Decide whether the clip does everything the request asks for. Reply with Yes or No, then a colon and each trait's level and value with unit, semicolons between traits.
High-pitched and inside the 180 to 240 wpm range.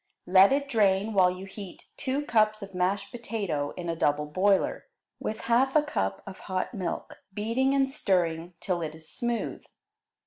No: high, 195 Hz; average, 170 wpm